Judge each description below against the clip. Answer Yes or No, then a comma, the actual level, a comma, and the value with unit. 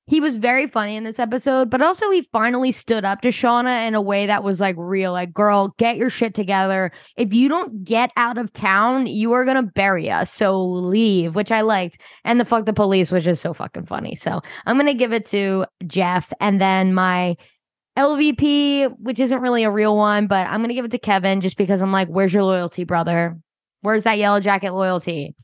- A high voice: Yes, high, 210 Hz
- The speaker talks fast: Yes, fast, 215 wpm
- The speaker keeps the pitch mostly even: No, average, 4.1 semitones